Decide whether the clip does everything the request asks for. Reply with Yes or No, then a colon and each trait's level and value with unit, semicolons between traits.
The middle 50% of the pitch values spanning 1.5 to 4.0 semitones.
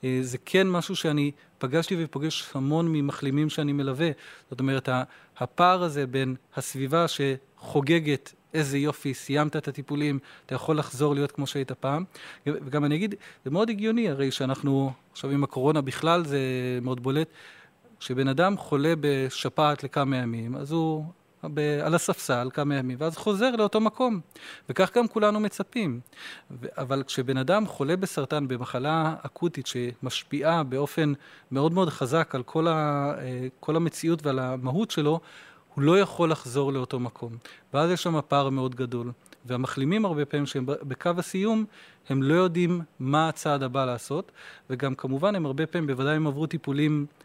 Yes: average, 3.6 semitones